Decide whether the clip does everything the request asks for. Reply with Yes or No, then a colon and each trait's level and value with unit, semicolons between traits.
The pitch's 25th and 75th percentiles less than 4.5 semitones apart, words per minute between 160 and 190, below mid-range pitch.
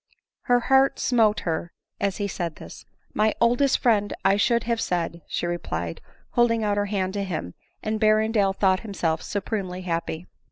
No: average, 4.0 semitones; average, 170 wpm; high, 205 Hz